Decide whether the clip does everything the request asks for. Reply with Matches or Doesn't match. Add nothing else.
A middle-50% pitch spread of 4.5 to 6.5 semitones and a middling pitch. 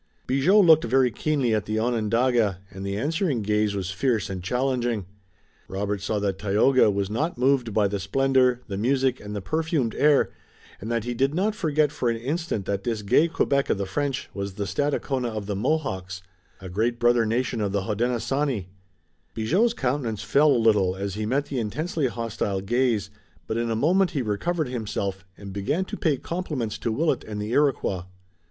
Doesn't match